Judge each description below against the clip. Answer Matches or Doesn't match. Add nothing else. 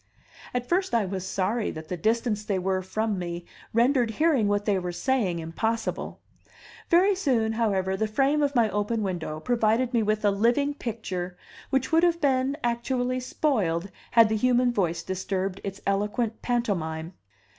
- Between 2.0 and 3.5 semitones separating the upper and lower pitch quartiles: Doesn't match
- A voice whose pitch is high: Matches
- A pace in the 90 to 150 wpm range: Doesn't match